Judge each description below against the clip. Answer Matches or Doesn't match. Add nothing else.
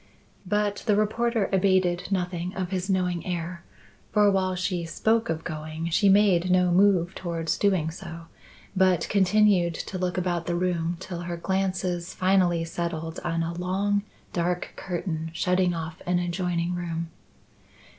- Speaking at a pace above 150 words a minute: Doesn't match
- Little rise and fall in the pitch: Matches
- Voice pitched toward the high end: Doesn't match